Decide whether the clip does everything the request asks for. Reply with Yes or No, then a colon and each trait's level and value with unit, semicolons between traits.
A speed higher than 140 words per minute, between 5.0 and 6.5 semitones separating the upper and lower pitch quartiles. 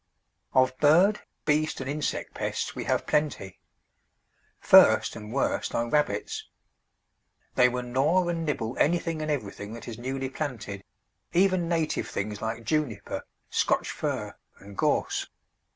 No: slow, 135 wpm; average, 5.3 semitones